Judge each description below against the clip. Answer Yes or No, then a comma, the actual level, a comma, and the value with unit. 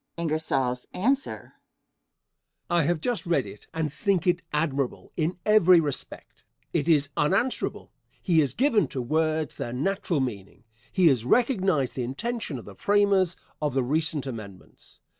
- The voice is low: No, medium, 160 Hz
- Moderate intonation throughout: No, wide, 5.8 semitones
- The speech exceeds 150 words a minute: No, average, 140 wpm